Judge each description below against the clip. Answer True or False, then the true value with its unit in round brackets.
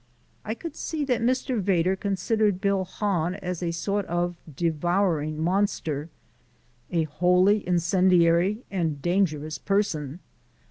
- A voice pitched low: False (180 Hz)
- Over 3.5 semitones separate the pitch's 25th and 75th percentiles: False (3.2 semitones)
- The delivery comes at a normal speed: False (120 wpm)